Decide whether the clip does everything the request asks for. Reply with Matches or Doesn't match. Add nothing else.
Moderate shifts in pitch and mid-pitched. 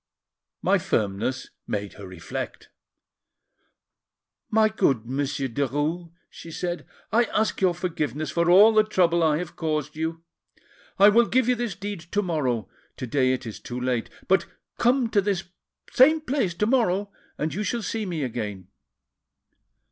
Doesn't match